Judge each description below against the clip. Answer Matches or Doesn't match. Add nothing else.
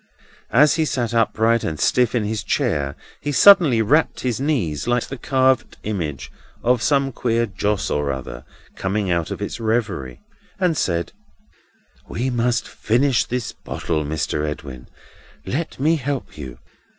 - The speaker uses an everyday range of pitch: Doesn't match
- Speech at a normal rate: Matches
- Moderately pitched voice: Doesn't match